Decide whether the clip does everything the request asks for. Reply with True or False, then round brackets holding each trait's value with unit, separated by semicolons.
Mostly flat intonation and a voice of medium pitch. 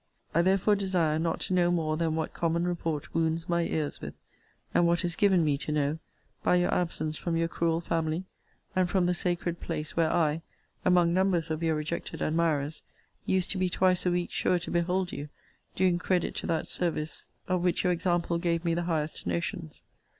True (1.9 semitones; 170 Hz)